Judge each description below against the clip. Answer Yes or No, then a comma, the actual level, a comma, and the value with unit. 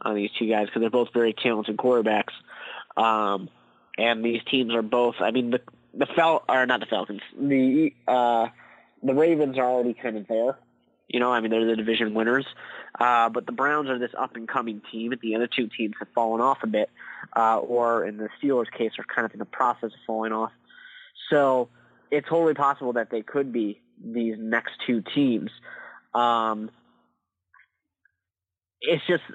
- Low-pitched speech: Yes, low, 115 Hz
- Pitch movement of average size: No, narrow, 2.2 semitones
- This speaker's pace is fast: No, average, 190 wpm